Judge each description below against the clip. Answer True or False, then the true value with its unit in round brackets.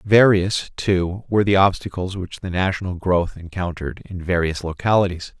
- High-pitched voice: False (90 Hz)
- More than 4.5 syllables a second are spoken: True (5.0 syllables/s)